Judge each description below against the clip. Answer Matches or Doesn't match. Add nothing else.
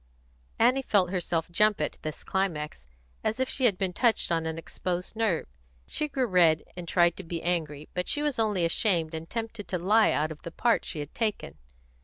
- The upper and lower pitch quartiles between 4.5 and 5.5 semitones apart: Matches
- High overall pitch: Doesn't match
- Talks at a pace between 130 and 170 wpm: Doesn't match